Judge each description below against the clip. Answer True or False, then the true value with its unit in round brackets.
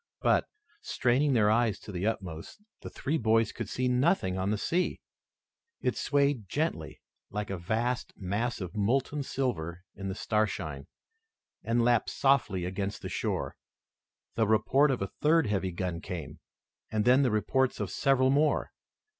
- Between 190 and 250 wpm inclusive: False (155 wpm)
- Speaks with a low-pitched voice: True (110 Hz)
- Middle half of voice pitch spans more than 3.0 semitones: True (5.3 semitones)